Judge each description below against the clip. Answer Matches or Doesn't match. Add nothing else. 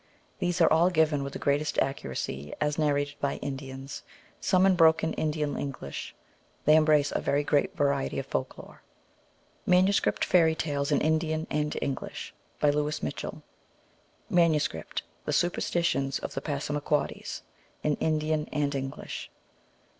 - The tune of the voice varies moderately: Doesn't match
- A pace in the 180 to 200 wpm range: Doesn't match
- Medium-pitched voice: Matches